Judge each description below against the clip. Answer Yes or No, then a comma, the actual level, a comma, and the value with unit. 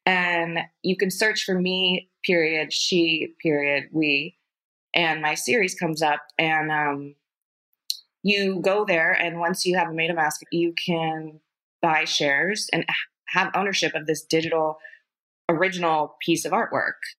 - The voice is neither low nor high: Yes, medium, 165 Hz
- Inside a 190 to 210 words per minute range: No, average, 145 wpm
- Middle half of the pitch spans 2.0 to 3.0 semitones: Yes, average, 2.7 semitones